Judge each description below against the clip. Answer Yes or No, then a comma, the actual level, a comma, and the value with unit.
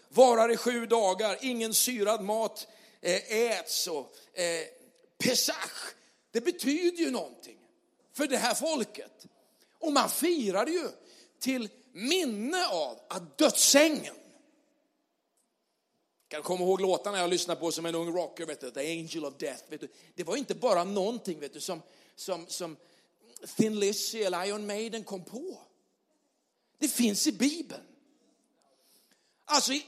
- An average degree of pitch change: No, wide, 7.9 semitones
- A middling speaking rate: Yes, average, 135 wpm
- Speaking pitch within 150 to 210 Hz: No, high, 230 Hz